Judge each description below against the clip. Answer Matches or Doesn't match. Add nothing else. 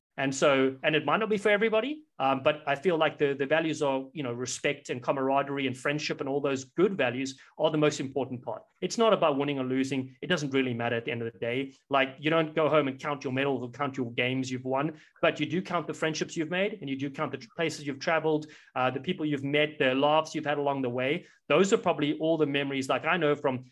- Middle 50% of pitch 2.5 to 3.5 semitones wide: Matches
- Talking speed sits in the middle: Doesn't match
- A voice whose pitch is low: Doesn't match